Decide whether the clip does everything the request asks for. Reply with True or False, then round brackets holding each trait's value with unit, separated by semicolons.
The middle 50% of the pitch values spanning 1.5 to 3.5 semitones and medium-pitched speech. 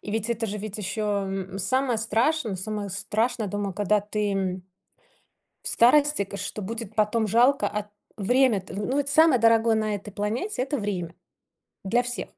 False (3.1 semitones; 215 Hz)